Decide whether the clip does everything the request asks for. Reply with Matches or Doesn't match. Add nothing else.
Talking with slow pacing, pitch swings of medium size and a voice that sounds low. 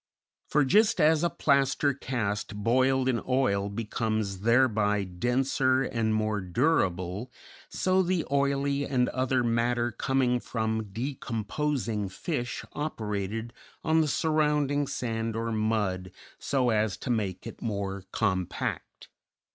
Matches